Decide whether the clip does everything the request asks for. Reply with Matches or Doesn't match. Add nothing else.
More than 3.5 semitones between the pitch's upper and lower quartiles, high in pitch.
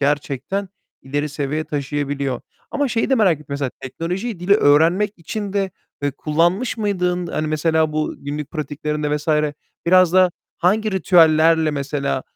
Doesn't match